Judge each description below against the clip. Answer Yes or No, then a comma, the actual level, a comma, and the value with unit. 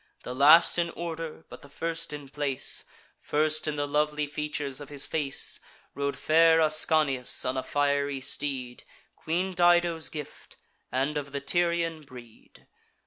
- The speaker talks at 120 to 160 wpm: Yes, average, 145 wpm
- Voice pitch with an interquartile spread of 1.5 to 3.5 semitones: Yes, narrow, 2.5 semitones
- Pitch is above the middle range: No, medium, 150 Hz